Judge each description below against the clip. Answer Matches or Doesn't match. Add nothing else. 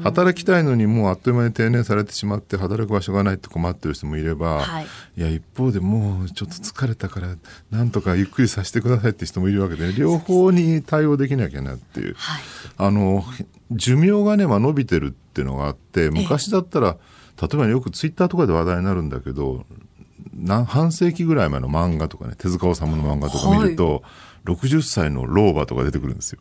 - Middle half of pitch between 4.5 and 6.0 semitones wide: Doesn't match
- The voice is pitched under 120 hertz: Matches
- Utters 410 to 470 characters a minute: Matches